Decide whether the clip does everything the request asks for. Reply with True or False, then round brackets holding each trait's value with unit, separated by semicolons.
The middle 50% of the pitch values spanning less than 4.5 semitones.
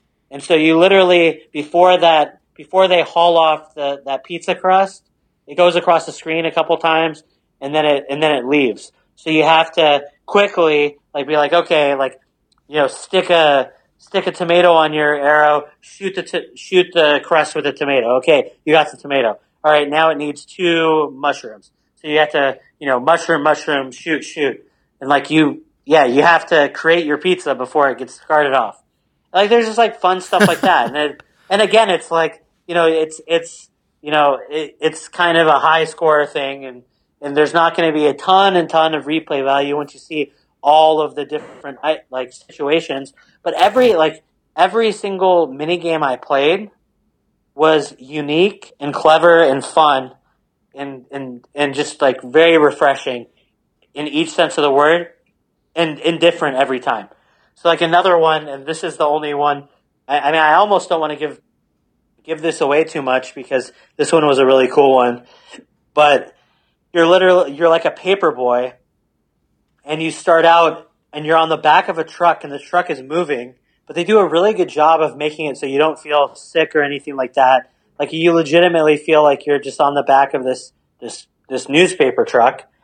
True (2.7 semitones)